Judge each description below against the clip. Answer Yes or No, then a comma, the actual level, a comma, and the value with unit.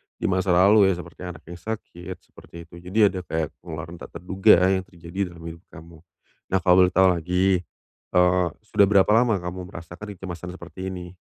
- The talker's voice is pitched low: Yes, very low, 90 Hz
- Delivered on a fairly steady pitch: Yes, narrow, 1.8 semitones